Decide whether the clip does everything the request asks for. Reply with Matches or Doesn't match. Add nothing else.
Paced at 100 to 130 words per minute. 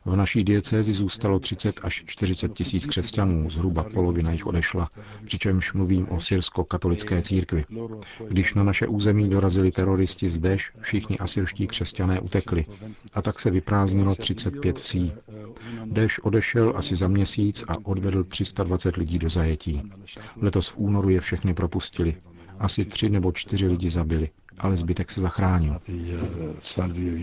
Doesn't match